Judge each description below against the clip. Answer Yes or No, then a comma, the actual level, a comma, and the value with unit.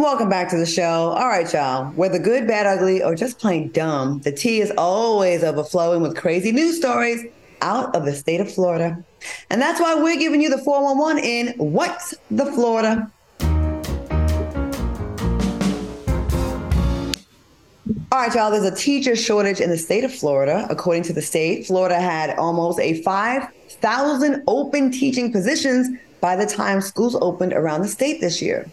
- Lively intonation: Yes, wide, 7.3 semitones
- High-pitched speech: Yes, high, 195 Hz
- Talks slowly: No, average, 160 wpm